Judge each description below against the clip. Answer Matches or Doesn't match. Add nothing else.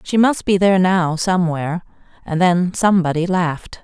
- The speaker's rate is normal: Matches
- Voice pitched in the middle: Matches